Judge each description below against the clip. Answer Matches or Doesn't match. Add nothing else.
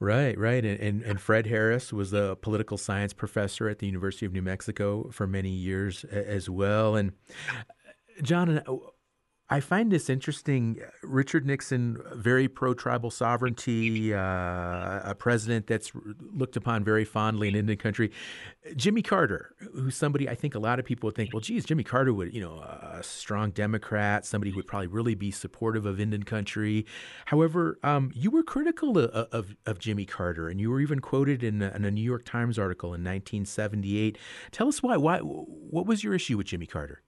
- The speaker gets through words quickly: Doesn't match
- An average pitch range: Matches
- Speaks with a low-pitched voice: Matches